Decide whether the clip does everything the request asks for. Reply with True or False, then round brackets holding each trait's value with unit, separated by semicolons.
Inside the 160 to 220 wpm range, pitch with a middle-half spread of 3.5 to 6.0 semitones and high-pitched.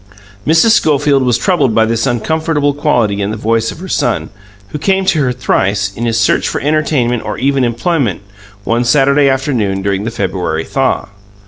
False (180 wpm; 4.9 semitones; 125 Hz)